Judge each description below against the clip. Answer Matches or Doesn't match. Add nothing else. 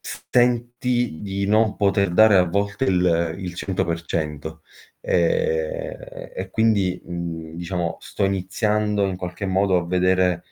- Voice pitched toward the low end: Matches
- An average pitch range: Matches